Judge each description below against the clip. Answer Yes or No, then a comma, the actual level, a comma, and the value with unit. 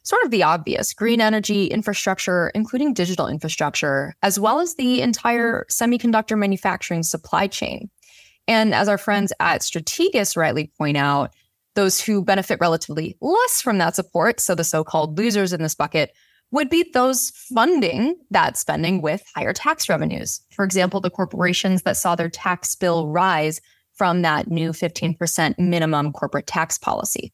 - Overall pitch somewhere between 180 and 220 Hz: Yes, high, 190 Hz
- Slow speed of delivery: No, average, 155 wpm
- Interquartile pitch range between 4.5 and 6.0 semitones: Yes, average, 5.0 semitones